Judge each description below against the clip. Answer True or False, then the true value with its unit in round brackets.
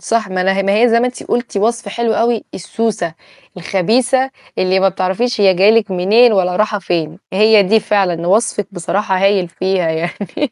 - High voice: True (200 Hz)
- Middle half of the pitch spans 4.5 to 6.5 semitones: False (3.6 semitones)